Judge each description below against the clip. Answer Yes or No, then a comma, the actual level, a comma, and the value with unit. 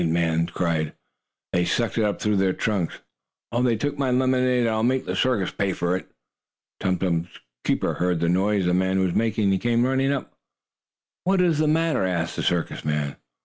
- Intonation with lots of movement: Yes, wide, 6.2 semitones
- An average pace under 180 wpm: No, average, 200 wpm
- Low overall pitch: Yes, low, 100 Hz